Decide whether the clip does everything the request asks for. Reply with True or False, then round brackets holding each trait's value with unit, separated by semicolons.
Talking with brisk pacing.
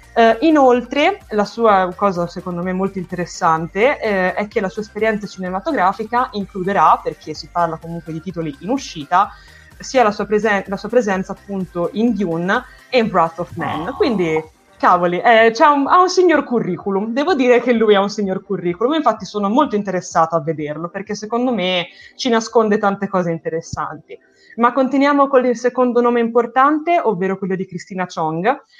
True (175 wpm)